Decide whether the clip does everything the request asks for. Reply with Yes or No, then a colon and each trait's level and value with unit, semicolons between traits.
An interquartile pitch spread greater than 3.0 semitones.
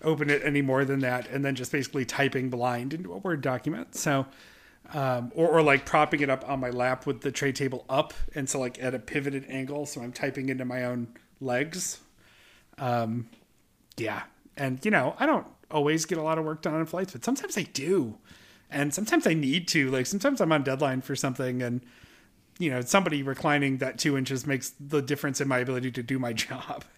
No: average, 2.7 semitones